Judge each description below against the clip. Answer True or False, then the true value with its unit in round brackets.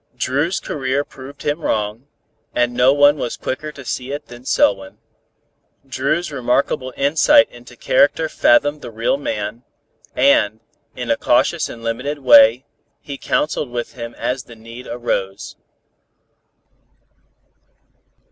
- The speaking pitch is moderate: False (130 Hz)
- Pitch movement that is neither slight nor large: True (3.4 semitones)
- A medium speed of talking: False (130 wpm)